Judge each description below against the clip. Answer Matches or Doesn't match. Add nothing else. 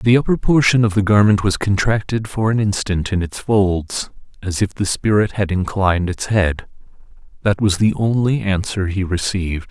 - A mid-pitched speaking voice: Doesn't match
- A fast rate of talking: Doesn't match